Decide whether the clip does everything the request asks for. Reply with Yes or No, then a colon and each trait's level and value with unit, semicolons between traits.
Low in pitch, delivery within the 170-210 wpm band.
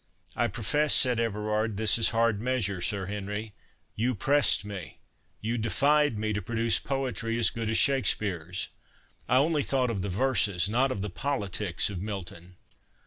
No: low, 110 Hz; average, 155 wpm